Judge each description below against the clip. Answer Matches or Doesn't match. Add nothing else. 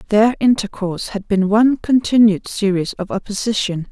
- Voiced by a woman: Matches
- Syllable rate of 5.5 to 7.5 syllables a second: Doesn't match